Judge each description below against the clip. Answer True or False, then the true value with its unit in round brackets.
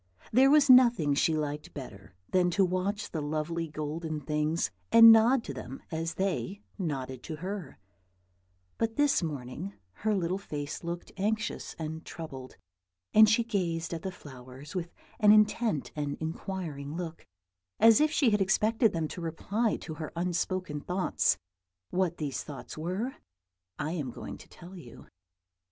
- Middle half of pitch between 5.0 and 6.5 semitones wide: True (5.3 semitones)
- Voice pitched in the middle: True (170 Hz)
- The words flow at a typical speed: True (155 wpm)